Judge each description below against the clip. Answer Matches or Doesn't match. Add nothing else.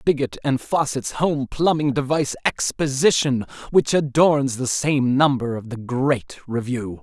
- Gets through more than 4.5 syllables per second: Doesn't match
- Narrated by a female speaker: Doesn't match